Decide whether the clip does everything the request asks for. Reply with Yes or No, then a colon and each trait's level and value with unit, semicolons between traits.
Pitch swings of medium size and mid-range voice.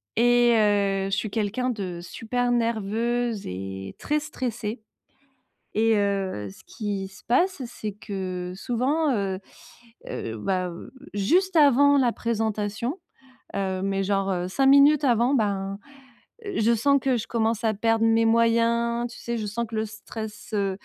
No: average, 3.5 semitones; high, 220 Hz